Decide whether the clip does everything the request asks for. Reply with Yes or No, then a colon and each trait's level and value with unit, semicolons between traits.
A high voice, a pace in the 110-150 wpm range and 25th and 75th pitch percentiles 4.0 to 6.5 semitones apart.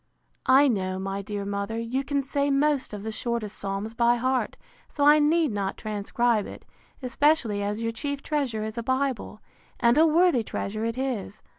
No: high, 235 Hz; average, 180 wpm; average, 4.9 semitones